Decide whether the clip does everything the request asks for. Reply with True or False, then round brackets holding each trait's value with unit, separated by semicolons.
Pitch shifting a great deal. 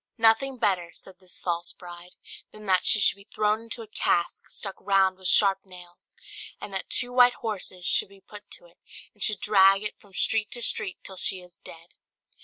False (2.7 semitones)